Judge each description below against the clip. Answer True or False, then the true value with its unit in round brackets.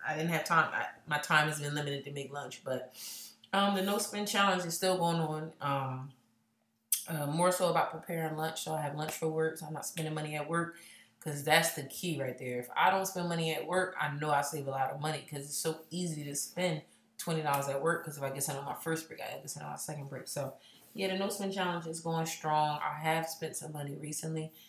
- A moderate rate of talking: False (255 wpm)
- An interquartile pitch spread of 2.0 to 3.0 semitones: True (2.7 semitones)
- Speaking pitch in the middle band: True (155 Hz)